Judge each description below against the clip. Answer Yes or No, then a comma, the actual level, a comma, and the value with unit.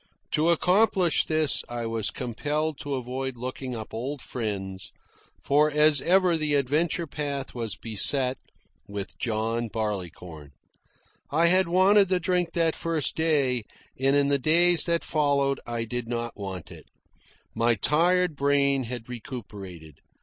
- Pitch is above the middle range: No, medium, 140 Hz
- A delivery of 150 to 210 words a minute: No, average, 140 wpm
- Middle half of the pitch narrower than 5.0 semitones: No, wide, 5.5 semitones